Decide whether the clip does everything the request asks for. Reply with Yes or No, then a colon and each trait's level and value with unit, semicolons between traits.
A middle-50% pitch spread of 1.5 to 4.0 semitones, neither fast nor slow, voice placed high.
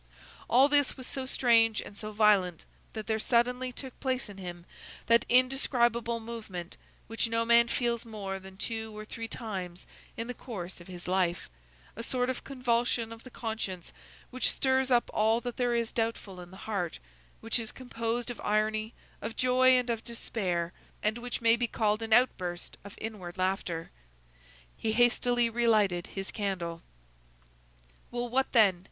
Yes: average, 3.6 semitones; average, 165 wpm; high, 225 Hz